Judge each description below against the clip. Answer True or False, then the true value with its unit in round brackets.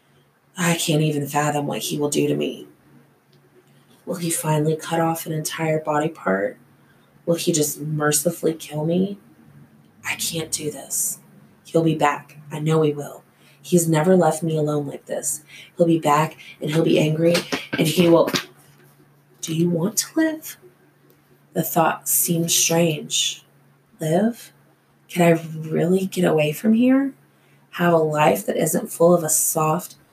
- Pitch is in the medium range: True (160 Hz)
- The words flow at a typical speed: True (155 wpm)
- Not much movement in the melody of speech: True (2.2 semitones)